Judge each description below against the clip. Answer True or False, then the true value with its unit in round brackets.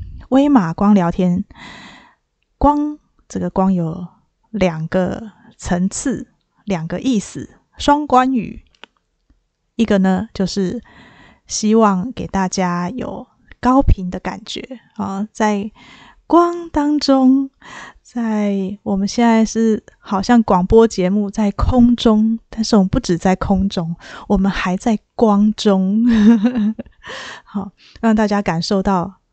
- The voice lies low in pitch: False (210 Hz)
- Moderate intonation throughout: True (3.9 semitones)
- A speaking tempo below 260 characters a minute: True (165 characters per minute)